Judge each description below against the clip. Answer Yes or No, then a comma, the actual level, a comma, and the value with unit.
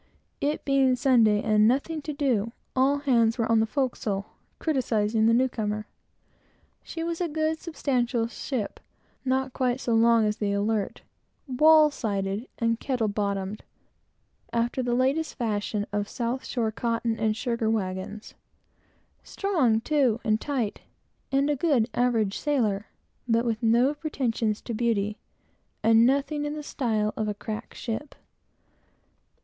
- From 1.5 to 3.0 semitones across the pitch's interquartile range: No, average, 3.9 semitones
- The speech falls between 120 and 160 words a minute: Yes, average, 145 wpm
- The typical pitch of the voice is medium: No, high, 235 Hz